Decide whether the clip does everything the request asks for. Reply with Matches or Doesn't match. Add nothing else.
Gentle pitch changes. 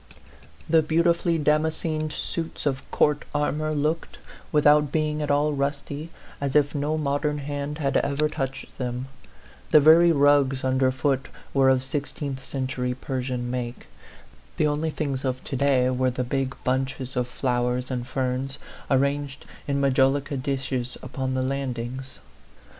Matches